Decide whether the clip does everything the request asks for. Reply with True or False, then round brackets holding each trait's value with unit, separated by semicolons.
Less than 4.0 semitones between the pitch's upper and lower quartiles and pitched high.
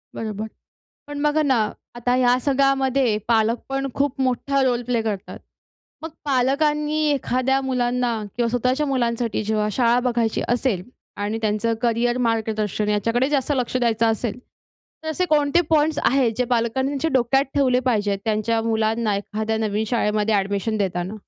True (3.4 semitones; 240 Hz)